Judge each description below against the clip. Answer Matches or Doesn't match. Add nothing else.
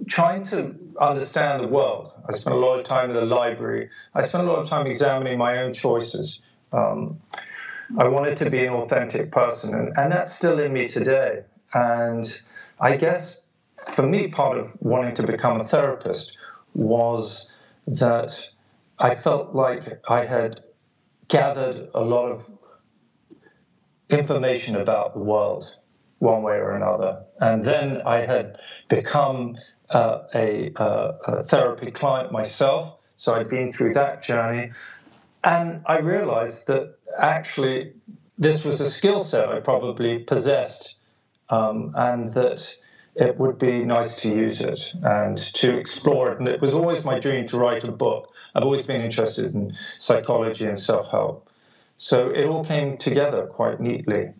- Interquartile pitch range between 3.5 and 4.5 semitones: Matches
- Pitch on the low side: Matches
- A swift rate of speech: Doesn't match